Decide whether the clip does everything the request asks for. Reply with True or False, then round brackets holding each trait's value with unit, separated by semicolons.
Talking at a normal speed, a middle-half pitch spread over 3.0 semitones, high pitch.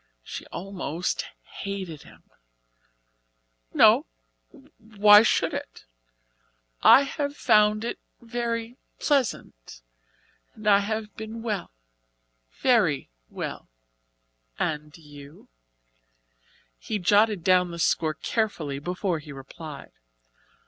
False (95 wpm; 5.6 semitones; 200 Hz)